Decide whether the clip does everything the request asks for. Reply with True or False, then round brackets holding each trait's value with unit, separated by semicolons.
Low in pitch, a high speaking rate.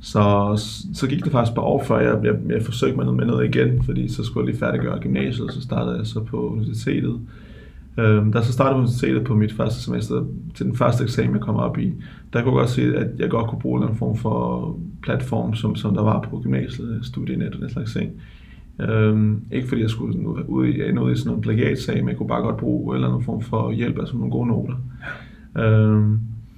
True (105 Hz; 235 wpm)